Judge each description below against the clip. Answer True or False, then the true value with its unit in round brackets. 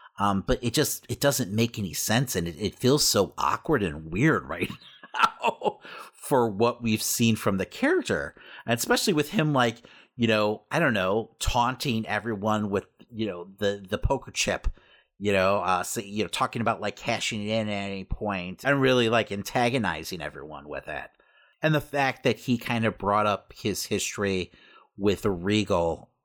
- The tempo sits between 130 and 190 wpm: True (185 wpm)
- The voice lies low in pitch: True (110 Hz)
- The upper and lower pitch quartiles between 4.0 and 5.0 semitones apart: False (3.4 semitones)